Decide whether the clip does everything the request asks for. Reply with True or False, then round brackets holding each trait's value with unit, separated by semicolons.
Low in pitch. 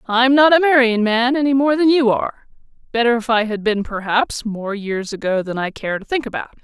False (235 Hz)